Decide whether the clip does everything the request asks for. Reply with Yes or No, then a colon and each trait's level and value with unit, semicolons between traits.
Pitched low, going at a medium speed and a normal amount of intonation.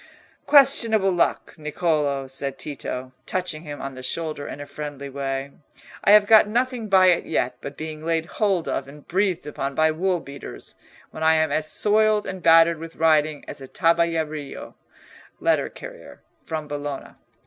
No: medium, 160 Hz; average, 165 wpm; average, 4.4 semitones